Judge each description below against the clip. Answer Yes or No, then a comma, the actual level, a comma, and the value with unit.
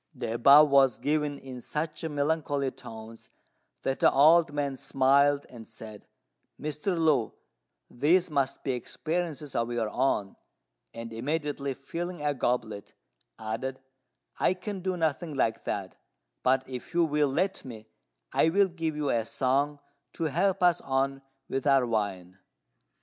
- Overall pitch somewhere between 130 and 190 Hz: Yes, medium, 140 Hz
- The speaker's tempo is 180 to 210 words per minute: No, average, 145 wpm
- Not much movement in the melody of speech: No, average, 4.2 semitones